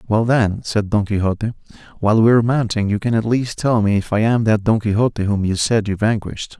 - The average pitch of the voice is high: No, low, 110 Hz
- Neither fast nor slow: No, fast, 235 wpm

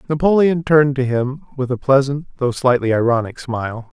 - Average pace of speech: Yes, average, 165 wpm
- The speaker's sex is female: No, male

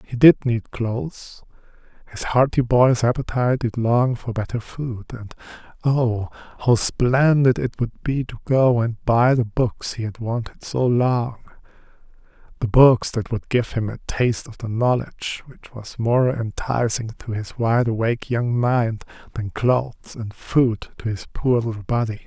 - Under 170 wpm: Yes, average, 160 wpm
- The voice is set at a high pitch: No, low, 120 Hz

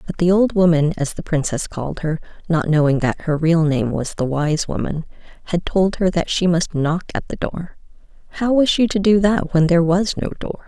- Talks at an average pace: No, fast, 215 wpm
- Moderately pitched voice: Yes, medium, 170 Hz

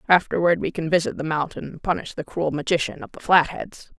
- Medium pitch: Yes, medium, 165 Hz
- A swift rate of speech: Yes, fast, 210 wpm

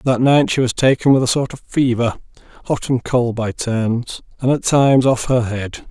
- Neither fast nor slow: No, fast, 215 wpm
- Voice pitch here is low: Yes, low, 125 Hz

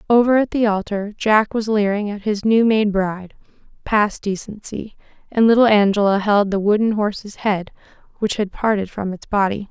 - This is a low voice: No, high, 210 Hz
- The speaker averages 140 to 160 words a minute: No, average, 175 wpm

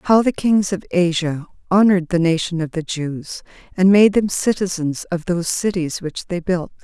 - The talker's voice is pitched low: No, medium, 180 Hz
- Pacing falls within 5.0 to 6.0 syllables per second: No, 4.8 syllables/s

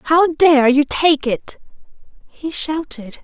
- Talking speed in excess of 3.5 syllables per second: No, 3.2 syllables/s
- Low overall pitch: No, very high, 295 Hz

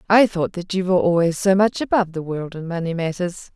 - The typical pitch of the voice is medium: Yes, medium, 180 Hz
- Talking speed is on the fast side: Yes, fast, 235 wpm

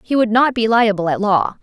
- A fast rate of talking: Yes, fast, 260 wpm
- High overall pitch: Yes, high, 215 Hz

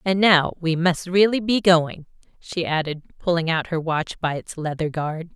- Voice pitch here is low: No, medium, 170 Hz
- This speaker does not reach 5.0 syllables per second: Yes, 4.5 syllables/s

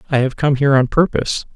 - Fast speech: Yes, fast, 230 wpm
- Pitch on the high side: No, medium, 140 Hz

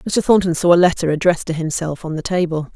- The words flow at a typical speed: No, fast, 240 wpm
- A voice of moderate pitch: Yes, medium, 170 Hz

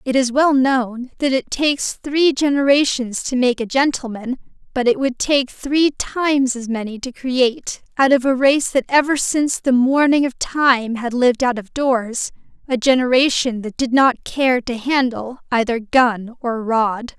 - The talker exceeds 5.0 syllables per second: No, 4.4 syllables/s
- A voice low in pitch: No, very high, 255 Hz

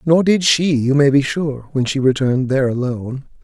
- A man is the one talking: Yes, male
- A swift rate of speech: Yes, fast, 210 wpm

